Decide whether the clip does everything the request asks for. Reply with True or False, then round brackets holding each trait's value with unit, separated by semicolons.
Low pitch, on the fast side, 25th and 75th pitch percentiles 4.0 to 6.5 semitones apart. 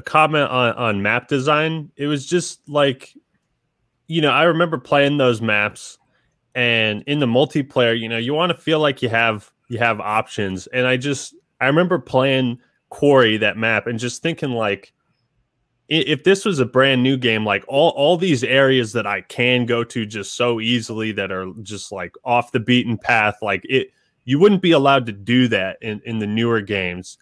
False (125 Hz; 195 wpm; 4.4 semitones)